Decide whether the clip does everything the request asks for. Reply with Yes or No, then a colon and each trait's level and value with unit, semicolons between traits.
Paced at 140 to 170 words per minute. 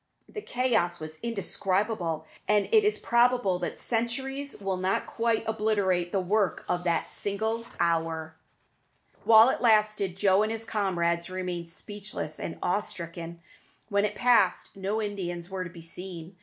Yes: average, 150 wpm